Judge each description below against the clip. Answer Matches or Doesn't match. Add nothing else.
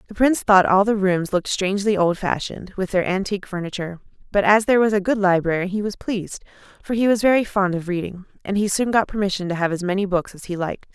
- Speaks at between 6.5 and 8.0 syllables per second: Matches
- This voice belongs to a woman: Matches